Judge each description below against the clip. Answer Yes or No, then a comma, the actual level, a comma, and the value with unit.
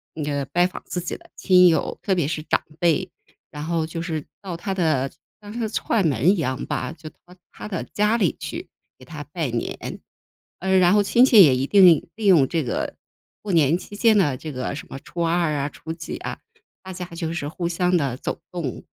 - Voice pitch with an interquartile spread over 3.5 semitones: Yes, average, 4.0 semitones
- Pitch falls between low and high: Yes, medium, 170 Hz